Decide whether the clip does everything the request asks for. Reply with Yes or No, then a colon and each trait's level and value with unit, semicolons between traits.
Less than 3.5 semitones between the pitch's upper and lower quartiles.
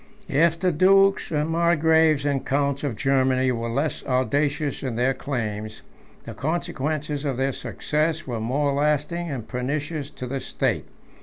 Yes: average, 3.1 semitones